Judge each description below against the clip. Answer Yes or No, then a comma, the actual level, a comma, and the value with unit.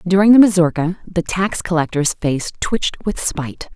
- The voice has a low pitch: No, medium, 175 Hz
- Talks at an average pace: Yes, average, 160 wpm